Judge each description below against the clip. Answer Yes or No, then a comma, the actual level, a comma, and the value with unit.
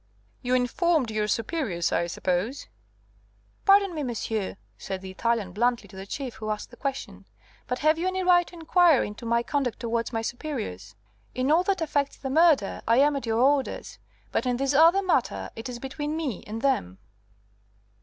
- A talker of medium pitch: No, very high, 255 Hz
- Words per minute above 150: Yes, average, 185 wpm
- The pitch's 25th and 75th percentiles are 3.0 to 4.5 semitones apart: No, wide, 5.6 semitones